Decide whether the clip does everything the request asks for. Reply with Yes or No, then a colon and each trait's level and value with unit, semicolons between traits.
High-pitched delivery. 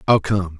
No: very low, 95 Hz